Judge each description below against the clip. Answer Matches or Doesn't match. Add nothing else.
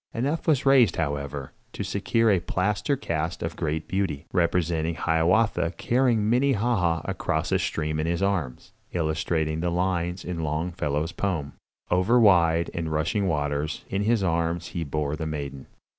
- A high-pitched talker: Doesn't match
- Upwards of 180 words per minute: Doesn't match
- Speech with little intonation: Doesn't match